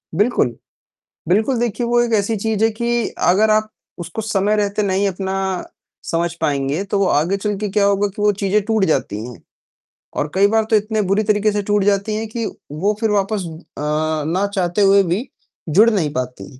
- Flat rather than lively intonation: No, average, 3.4 semitones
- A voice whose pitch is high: Yes, high, 200 Hz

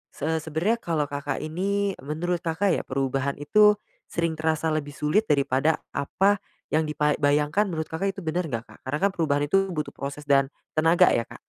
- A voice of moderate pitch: Yes, medium, 155 Hz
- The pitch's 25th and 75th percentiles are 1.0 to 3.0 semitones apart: No, average, 3.5 semitones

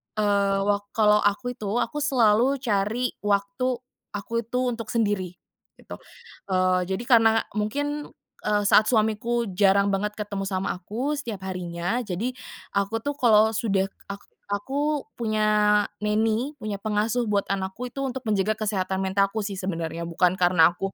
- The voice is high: Yes, high, 210 Hz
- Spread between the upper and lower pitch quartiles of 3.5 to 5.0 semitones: No, average, 2.9 semitones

